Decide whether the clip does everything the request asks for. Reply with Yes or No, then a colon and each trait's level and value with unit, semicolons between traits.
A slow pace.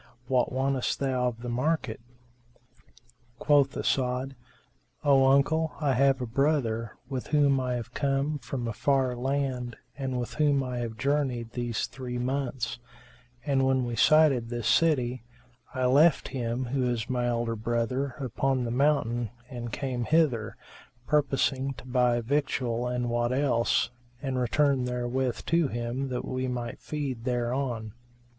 No: average, 145 wpm